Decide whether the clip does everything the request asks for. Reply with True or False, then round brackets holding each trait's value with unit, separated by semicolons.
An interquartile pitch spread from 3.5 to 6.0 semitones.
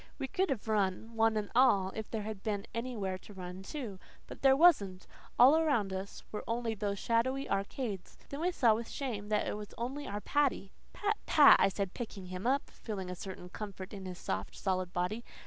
True (4.5 semitones)